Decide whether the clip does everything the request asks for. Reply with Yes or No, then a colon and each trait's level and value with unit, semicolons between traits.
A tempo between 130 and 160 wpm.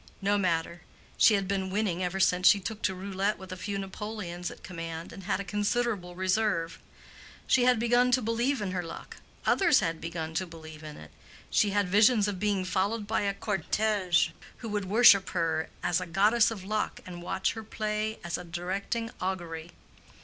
No: average, 190 wpm